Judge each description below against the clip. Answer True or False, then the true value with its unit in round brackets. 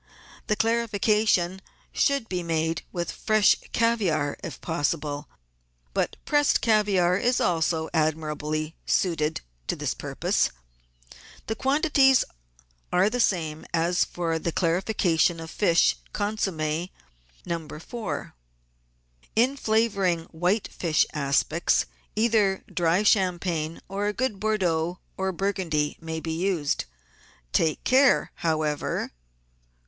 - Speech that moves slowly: True (115 wpm)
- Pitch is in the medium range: True (175 Hz)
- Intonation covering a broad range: False (4.8 semitones)